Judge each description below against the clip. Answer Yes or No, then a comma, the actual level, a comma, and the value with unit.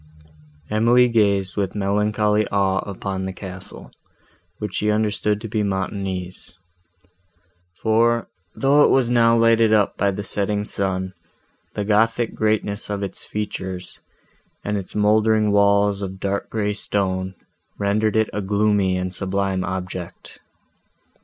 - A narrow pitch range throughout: Yes, narrow, 2.0 semitones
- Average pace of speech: No, slow, 130 wpm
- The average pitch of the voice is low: Yes, low, 100 Hz